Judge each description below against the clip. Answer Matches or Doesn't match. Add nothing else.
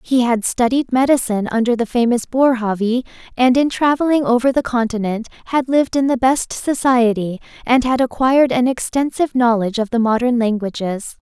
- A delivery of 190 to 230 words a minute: Doesn't match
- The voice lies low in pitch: Doesn't match